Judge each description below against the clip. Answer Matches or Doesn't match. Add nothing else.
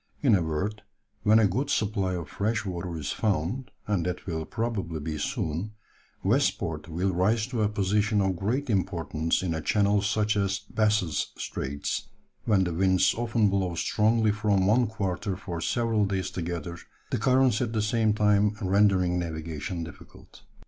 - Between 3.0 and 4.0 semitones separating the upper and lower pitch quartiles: Matches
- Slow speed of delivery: Doesn't match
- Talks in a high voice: Doesn't match